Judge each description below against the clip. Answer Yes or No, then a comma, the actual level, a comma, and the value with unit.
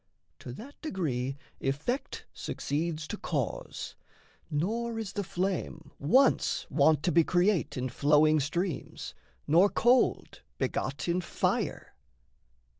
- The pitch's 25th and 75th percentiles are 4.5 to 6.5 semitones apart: Yes, average, 5.2 semitones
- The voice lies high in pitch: No, medium, 170 Hz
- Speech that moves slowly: Yes, slow, 115 wpm